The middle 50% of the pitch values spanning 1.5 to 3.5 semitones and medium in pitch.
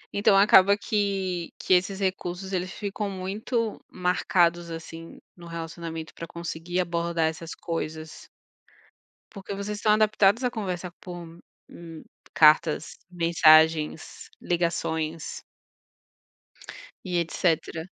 Yes: average, 2.9 semitones; medium, 175 Hz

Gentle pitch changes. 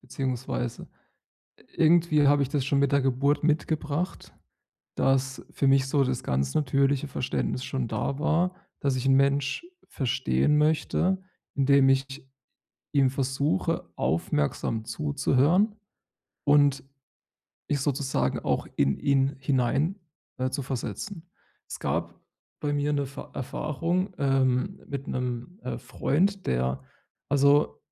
Yes: narrow, 2.3 semitones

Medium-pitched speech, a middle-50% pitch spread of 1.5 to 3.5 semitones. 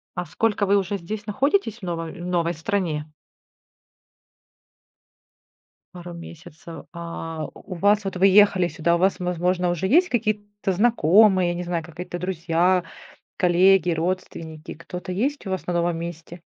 Yes: medium, 180 Hz; average, 2.8 semitones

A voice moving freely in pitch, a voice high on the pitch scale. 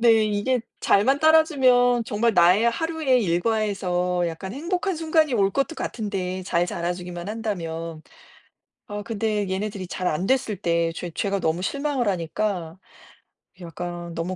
Yes: wide, 5.7 semitones; high, 205 Hz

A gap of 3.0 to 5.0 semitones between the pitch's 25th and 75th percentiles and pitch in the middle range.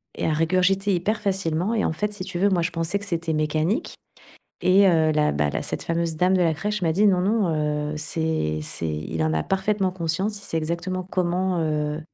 Yes: average, 3.5 semitones; medium, 170 Hz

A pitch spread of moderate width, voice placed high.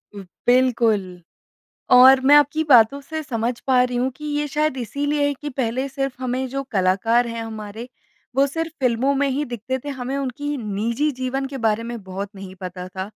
Yes: average, 3.7 semitones; very high, 255 Hz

